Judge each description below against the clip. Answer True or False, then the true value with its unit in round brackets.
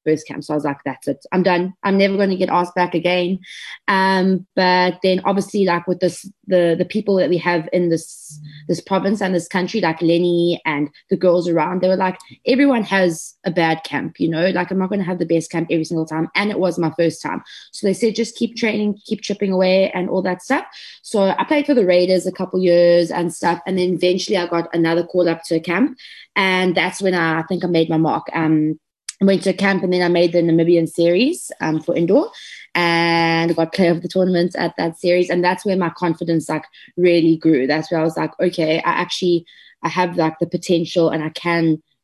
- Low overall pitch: False (175 Hz)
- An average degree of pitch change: False (2.2 semitones)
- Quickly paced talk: True (235 wpm)